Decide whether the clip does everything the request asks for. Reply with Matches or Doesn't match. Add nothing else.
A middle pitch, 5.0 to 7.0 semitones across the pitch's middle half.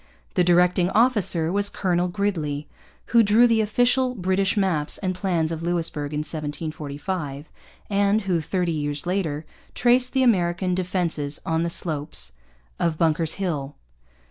Doesn't match